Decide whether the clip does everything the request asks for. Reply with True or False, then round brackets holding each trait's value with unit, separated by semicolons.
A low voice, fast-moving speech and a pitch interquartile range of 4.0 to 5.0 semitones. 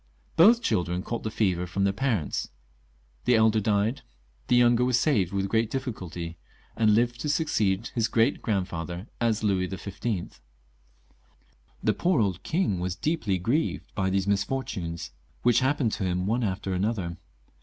False (105 Hz; 155 wpm; 4.5 semitones)